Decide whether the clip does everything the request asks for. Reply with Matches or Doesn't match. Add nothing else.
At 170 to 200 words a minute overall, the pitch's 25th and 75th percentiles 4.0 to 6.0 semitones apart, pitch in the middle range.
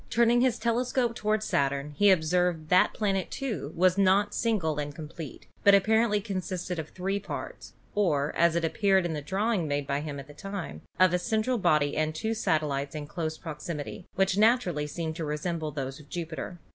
Matches